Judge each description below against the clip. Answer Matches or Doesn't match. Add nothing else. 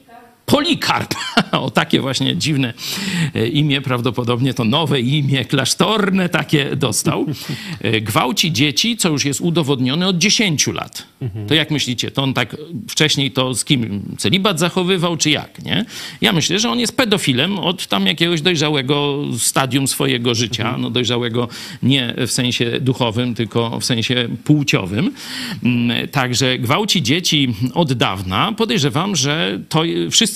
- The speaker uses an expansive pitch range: Matches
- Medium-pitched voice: Matches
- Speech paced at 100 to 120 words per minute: Doesn't match